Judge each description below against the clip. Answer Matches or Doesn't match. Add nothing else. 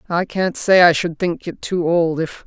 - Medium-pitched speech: Matches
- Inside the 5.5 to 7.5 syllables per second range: Doesn't match